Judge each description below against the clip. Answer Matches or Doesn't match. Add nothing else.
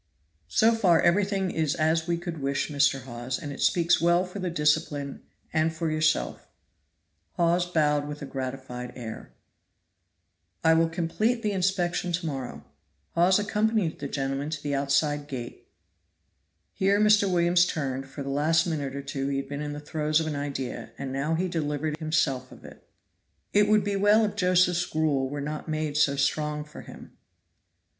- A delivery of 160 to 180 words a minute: Matches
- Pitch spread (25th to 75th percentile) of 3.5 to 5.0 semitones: Matches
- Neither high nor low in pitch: Matches